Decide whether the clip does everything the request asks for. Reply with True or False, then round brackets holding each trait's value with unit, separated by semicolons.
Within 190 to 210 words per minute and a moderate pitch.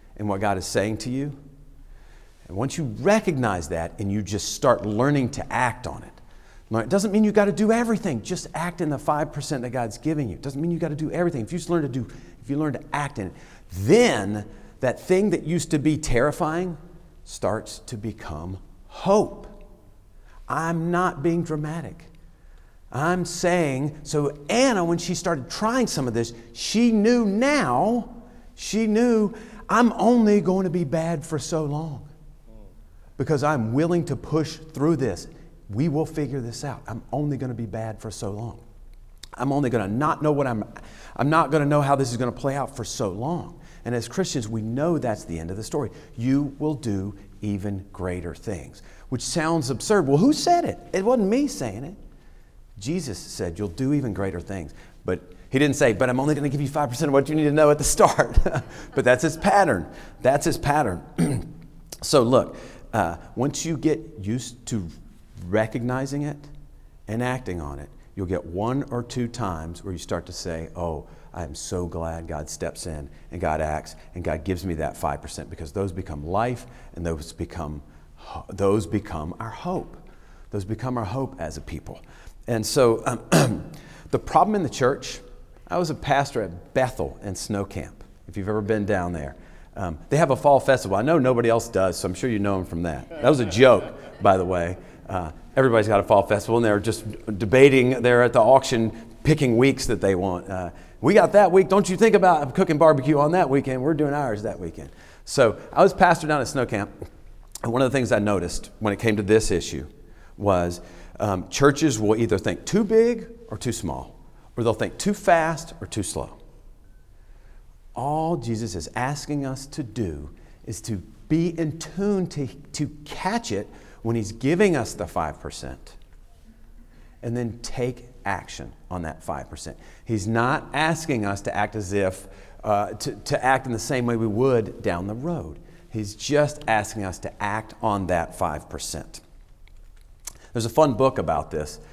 False (195 wpm; 120 Hz)